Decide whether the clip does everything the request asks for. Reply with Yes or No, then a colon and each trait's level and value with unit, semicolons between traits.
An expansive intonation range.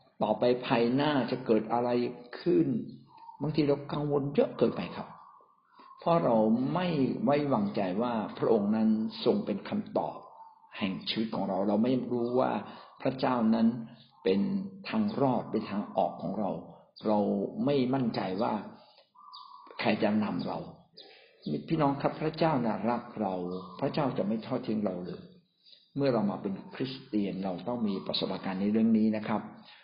Yes: wide, 6.0 semitones